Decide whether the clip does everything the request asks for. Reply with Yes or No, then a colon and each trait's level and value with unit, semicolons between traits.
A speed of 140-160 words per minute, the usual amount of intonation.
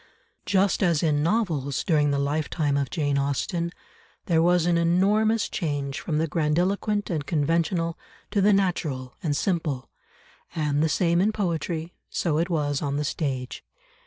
Yes: average, 155 wpm; average, 3.5 semitones